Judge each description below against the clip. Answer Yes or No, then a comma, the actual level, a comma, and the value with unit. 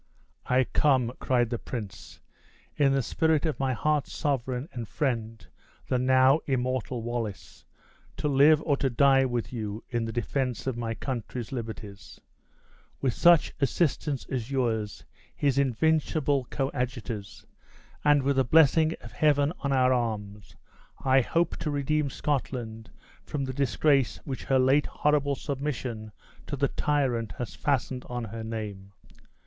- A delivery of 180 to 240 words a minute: No, average, 145 wpm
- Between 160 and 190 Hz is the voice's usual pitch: No, low, 130 Hz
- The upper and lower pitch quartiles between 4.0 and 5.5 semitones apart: No, average, 3.5 semitones